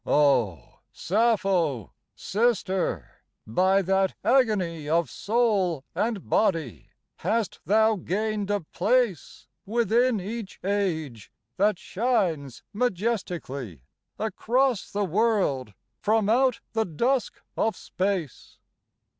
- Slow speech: Yes, slow, 95 wpm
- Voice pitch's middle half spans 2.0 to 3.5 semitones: No, average, 5.1 semitones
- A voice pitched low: No, high, 200 Hz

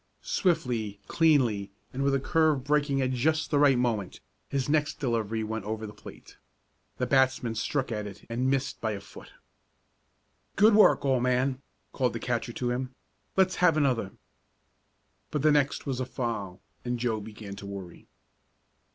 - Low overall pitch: Yes, low, 125 Hz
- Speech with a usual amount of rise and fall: Yes, average, 4.3 semitones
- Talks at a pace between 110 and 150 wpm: No, average, 165 wpm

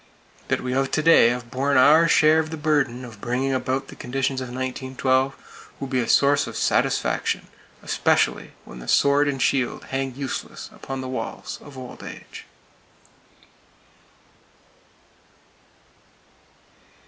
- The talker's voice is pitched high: No, low, 135 Hz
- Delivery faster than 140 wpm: No, slow, 135 wpm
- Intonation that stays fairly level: Yes, narrow, 1.7 semitones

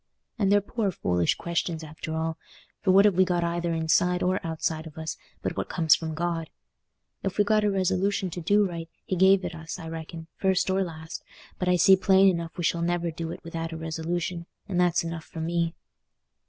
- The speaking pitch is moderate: Yes, medium, 170 Hz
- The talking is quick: Yes, fast, 210 wpm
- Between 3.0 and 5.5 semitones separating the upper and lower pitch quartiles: No, narrow, 2.4 semitones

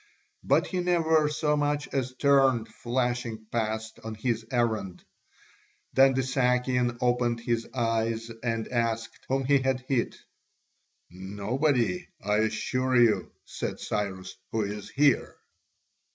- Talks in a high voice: No, low, 120 Hz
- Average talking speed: No, slow, 125 wpm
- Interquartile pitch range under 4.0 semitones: Yes, average, 3.0 semitones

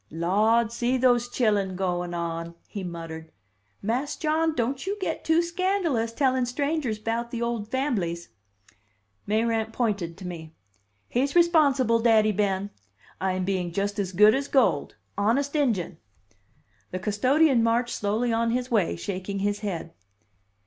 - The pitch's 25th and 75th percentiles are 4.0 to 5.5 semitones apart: Yes, average, 5.2 semitones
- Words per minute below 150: Yes, average, 140 wpm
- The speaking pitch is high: Yes, high, 225 Hz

